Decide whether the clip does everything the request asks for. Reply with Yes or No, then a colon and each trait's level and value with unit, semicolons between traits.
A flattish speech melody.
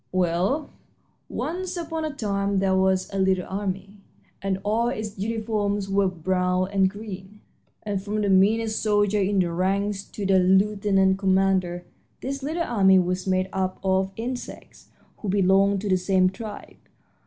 Yes: narrow, 1.9 semitones